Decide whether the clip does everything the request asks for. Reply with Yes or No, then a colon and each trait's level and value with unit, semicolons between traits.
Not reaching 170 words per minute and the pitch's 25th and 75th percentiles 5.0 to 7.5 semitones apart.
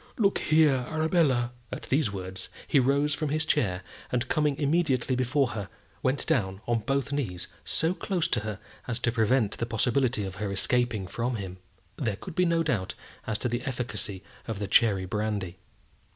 No: average, 180 wpm; wide, 5.4 semitones